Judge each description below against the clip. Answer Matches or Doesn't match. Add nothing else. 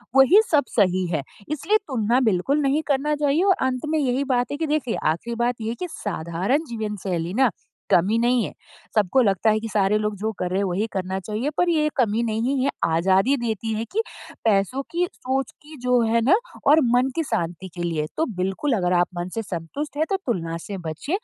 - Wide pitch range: Matches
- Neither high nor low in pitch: Doesn't match